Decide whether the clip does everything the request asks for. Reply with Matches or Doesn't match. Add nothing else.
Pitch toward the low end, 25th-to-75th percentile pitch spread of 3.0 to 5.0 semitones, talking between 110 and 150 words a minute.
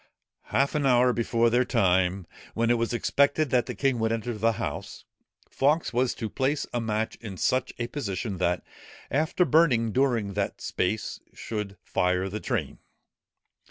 Doesn't match